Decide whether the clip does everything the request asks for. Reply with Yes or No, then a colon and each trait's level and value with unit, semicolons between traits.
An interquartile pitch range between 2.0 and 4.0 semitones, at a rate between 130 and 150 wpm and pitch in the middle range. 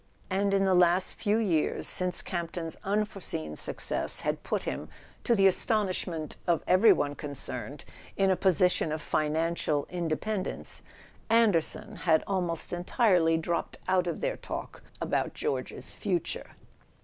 Yes: average, 3.3 semitones; slow, 135 wpm; medium, 180 Hz